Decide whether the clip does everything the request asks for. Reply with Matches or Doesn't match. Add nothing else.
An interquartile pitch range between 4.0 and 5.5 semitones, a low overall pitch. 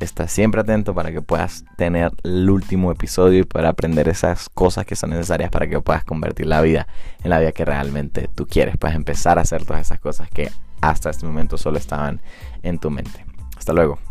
Doesn't match